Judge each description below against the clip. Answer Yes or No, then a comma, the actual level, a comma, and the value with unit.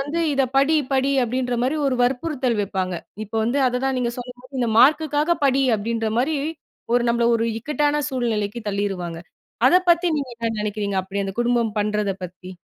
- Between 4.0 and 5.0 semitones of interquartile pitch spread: Yes, average, 4.5 semitones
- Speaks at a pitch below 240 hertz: No, high, 245 Hz